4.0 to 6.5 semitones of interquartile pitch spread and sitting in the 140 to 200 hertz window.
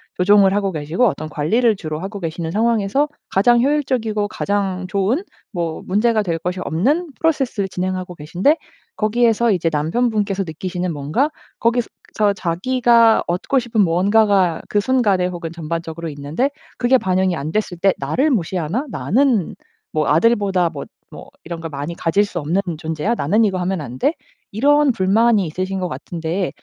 Yes: wide, 5.5 semitones; high, 190 Hz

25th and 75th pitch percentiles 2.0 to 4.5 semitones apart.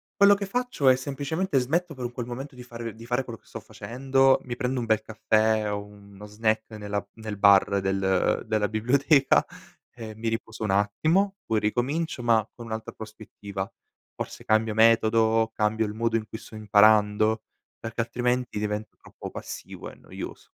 Yes: average, 2.7 semitones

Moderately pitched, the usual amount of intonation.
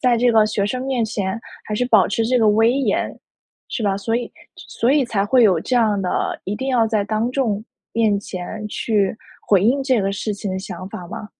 No: high, 220 Hz; average, 3.3 semitones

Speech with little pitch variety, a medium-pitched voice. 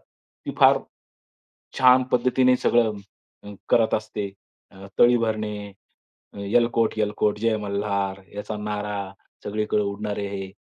No: narrow, 2.0 semitones; low, 105 Hz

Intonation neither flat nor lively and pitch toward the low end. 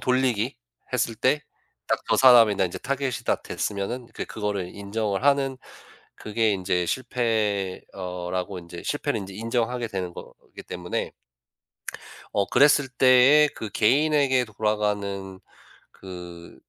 Yes: average, 4.8 semitones; low, 110 Hz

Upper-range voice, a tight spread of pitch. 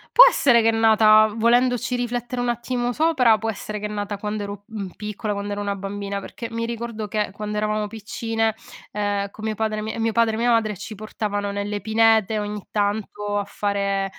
Yes: high, 215 Hz; narrow, 1.8 semitones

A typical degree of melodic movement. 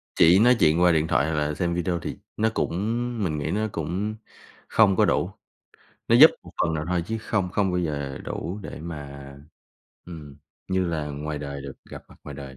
Yes: average, 4.0 semitones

